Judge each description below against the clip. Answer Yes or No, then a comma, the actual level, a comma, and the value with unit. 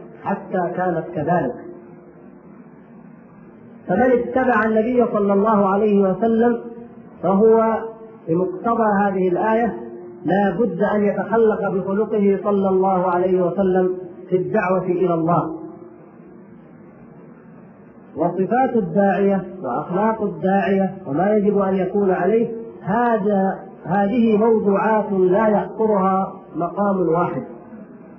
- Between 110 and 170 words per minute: No, average, 90 wpm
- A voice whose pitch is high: Yes, high, 200 Hz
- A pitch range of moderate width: Yes, average, 3.1 semitones